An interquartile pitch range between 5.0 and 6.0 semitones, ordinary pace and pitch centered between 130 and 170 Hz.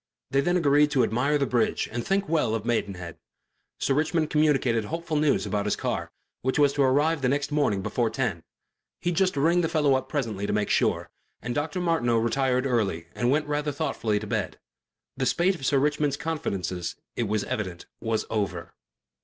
Yes: average, 5.3 semitones; average, 190 wpm; low, 135 Hz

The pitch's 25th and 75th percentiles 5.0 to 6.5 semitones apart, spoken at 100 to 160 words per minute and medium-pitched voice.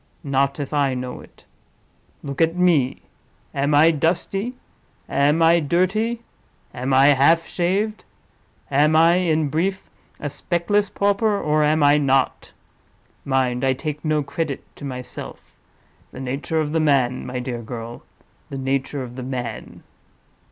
No: average, 3.9 semitones; average, 140 wpm; medium, 145 Hz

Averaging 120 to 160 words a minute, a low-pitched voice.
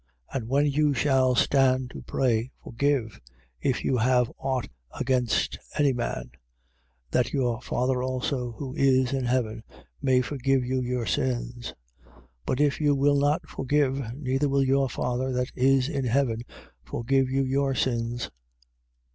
Yes: average, 150 wpm; low, 130 Hz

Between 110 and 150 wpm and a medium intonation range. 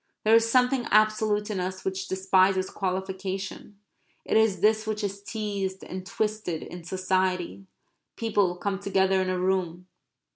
No: average, 145 wpm; narrow, 2.2 semitones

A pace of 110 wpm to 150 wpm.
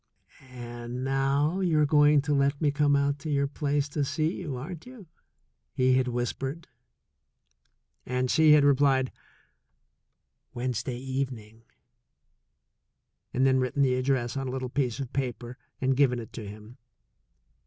Yes: average, 145 wpm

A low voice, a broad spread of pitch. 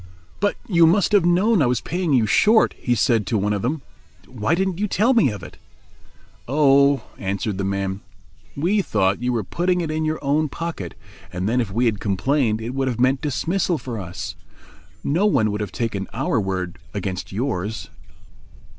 Yes: low, 125 Hz; wide, 8.1 semitones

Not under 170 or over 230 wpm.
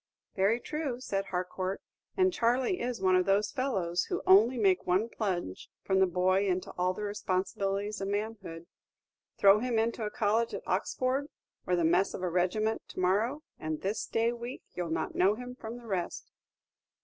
Yes: average, 180 wpm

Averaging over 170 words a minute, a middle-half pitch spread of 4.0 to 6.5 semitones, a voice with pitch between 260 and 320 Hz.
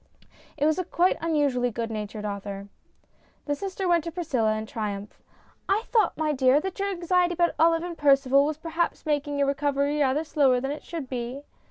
Yes: average, 195 wpm; average, 4.8 semitones; very high, 290 Hz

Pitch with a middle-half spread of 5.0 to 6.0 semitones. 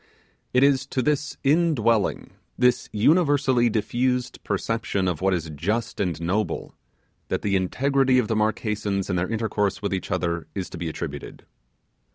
Yes: average, 5.3 semitones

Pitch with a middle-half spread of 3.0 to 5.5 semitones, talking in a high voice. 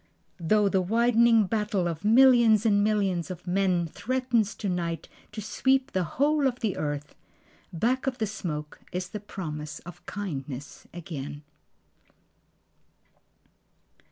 Yes: average, 5.1 semitones; high, 200 Hz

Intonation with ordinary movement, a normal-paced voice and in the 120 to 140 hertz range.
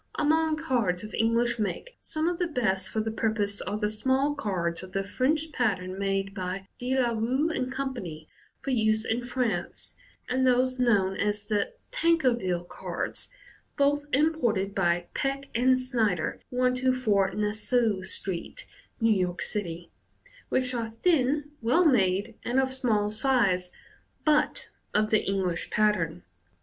No: average, 4.9 semitones; average, 150 wpm; high, 230 Hz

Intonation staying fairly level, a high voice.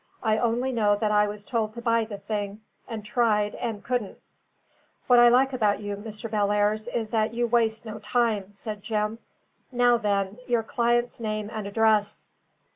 Yes: narrow, 2.2 semitones; high, 220 Hz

